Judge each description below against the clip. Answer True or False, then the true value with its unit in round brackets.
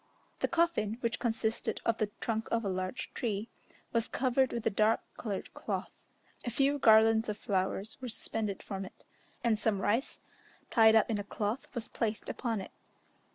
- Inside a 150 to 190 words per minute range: True (175 wpm)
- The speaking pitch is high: True (220 Hz)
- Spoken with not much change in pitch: True (2.2 semitones)